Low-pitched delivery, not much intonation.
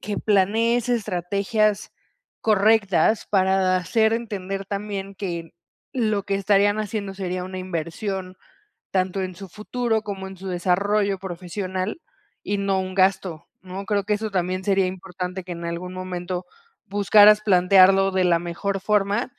No: high, 195 Hz; narrow, 2.0 semitones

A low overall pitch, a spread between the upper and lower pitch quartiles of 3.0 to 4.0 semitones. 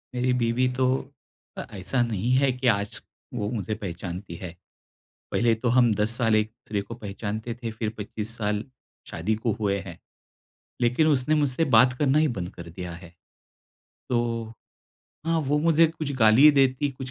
Yes: low, 115 Hz; average, 3.7 semitones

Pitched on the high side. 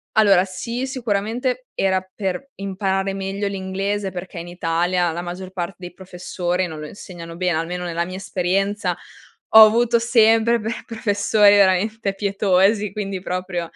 Yes: high, 195 Hz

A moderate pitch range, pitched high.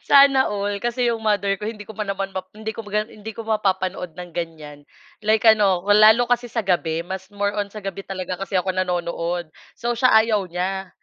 Yes: average, 3.1 semitones; high, 200 Hz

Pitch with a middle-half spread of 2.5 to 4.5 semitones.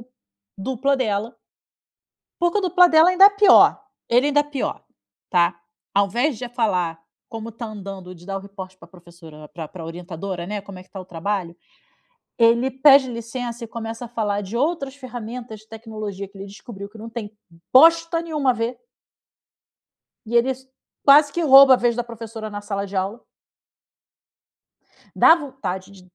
No: average, 5.0 semitones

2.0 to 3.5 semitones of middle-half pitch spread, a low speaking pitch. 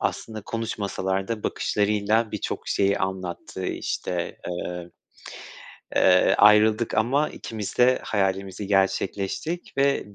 Yes: average, 2.7 semitones; low, 105 Hz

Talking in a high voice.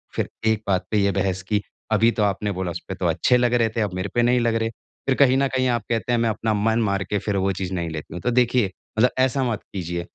No: low, 110 Hz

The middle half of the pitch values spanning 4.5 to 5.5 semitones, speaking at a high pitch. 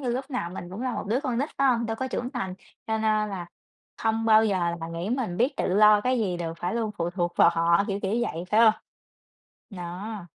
Yes: average, 4.8 semitones; high, 215 Hz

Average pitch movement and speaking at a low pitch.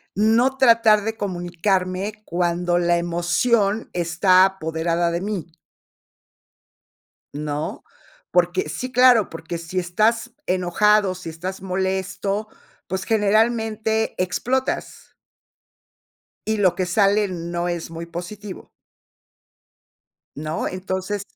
No: average, 3.5 semitones; medium, 185 Hz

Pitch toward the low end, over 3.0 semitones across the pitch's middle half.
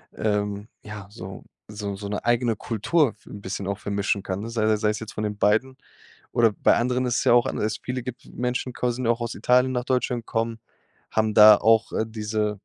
No: low, 110 Hz; average, 2.7 semitones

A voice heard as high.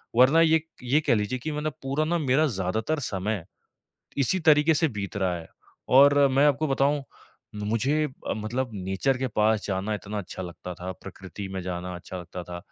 No: low, 115 Hz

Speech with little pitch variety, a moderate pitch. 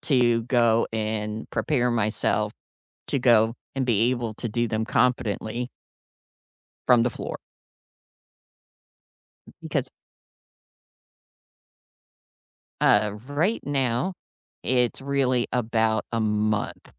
No: narrow, 2.3 semitones; low, 115 Hz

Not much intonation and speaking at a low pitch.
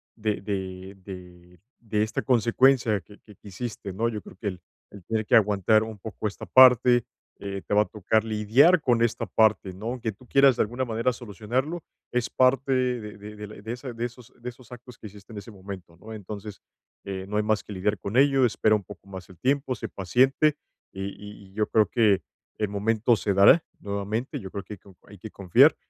No: average, 3.4 semitones; low, 105 Hz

